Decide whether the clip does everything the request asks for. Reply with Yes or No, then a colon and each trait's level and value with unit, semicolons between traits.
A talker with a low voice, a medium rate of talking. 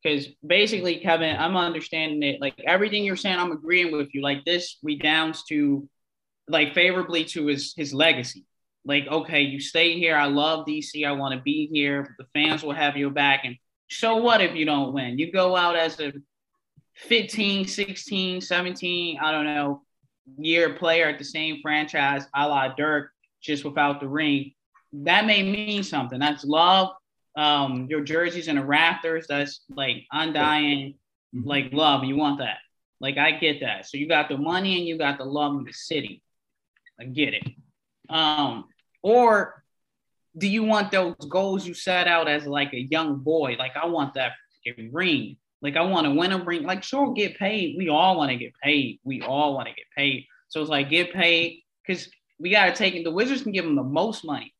No: medium, 155 Hz; average, 195 wpm